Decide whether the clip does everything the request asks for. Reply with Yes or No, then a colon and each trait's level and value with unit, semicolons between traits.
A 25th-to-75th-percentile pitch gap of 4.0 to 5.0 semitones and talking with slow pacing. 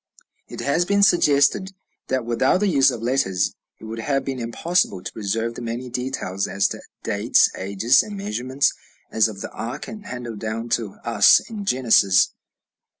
No: average, 4.3 semitones; average, 165 wpm